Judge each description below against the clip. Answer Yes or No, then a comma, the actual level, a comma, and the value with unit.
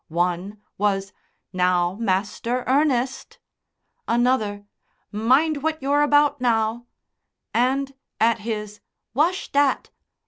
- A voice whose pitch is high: Yes, high, 235 Hz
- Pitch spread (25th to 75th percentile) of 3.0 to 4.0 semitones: No, average, 5.2 semitones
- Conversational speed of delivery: No, slow, 95 wpm